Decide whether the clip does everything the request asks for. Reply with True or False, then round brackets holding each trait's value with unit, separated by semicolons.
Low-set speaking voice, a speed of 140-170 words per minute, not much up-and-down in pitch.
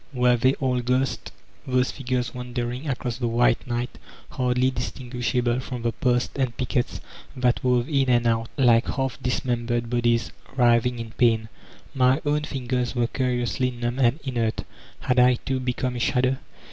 True (125 Hz; 160 wpm; 1.3 semitones)